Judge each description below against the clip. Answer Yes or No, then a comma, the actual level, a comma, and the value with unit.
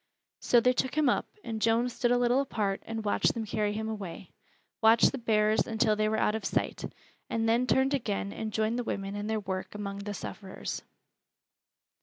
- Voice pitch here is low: No, high, 220 Hz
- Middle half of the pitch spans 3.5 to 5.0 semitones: No, narrow, 2.4 semitones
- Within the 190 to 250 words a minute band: Yes, average, 200 wpm